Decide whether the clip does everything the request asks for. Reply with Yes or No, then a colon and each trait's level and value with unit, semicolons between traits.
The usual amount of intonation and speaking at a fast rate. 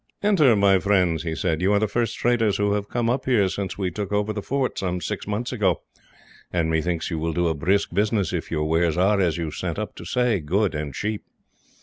Yes: average, 3.9 semitones; fast, 235 wpm